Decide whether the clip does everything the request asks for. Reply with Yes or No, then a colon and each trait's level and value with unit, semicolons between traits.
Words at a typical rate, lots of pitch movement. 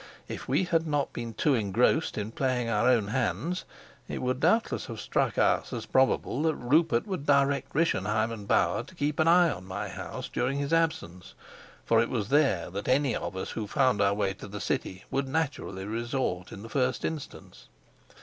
Yes: average, 195 wpm; wide, 5.8 semitones